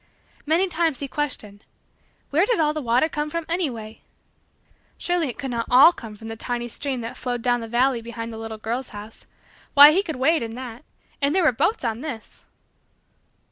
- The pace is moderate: Yes, average, 195 wpm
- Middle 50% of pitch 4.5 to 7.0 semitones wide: Yes, average, 5.2 semitones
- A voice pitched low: No, very high, 255 Hz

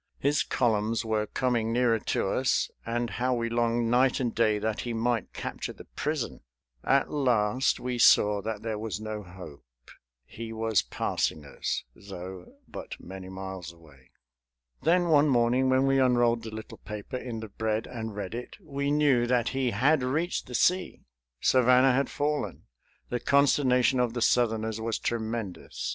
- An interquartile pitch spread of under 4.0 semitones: Yes, average, 3.0 semitones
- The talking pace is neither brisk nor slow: Yes, average, 165 wpm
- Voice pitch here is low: Yes, low, 115 Hz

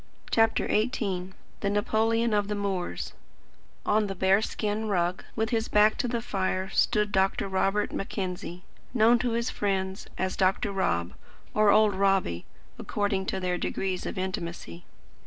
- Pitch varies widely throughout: No, narrow, 2.4 semitones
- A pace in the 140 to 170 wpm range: Yes, average, 150 wpm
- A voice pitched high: Yes, high, 200 Hz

